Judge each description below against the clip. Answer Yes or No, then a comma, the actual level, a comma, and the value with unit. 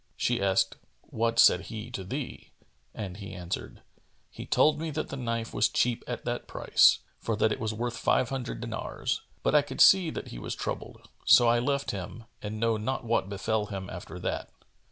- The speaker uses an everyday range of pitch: Yes, average, 3.4 semitones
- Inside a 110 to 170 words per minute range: No, average, 195 wpm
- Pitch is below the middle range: Yes, low, 115 Hz